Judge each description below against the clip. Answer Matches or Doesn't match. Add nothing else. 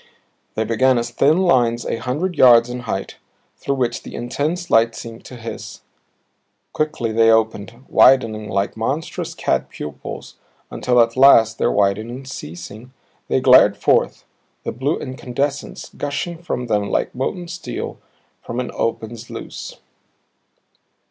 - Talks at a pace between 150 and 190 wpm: Doesn't match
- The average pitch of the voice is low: Matches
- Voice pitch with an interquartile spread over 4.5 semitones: Doesn't match